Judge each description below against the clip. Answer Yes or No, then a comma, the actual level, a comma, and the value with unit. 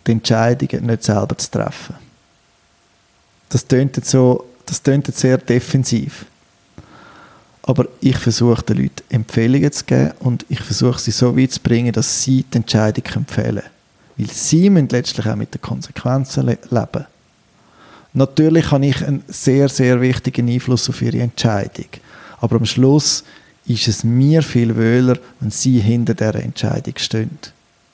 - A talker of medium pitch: No, low, 125 Hz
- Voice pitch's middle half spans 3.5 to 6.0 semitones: No, average, 2.8 semitones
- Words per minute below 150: Yes, average, 140 wpm